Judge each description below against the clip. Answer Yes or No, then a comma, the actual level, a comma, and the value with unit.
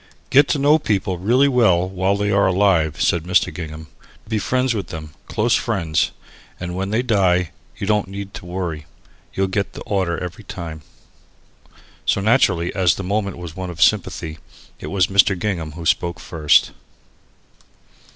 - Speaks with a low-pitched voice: Yes, very low, 95 Hz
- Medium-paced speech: Yes, average, 170 wpm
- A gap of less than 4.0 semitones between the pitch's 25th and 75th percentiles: Yes, average, 3.1 semitones